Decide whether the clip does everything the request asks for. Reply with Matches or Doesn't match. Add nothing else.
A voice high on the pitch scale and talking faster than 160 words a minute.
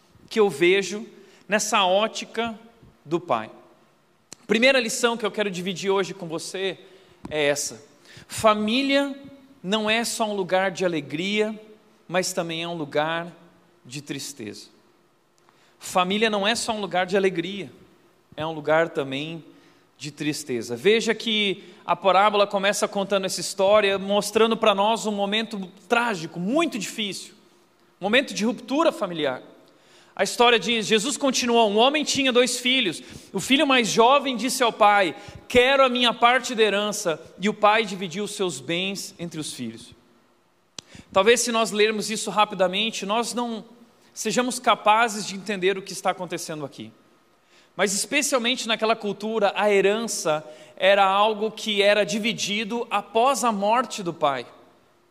Doesn't match